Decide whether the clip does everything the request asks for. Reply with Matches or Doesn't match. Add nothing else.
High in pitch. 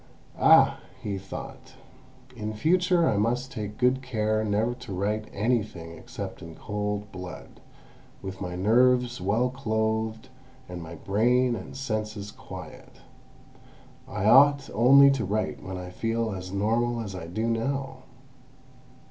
Doesn't match